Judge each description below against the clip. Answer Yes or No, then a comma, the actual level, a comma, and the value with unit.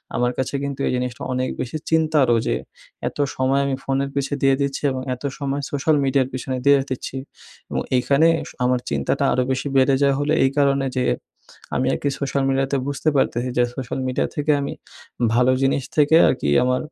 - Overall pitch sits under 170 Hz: Yes, low, 135 Hz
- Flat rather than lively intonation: Yes, narrow, 1.7 semitones